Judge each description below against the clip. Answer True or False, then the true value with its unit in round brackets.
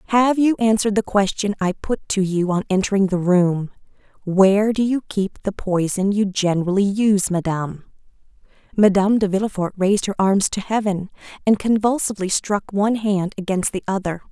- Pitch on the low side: False (200 Hz)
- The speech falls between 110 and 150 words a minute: False (160 wpm)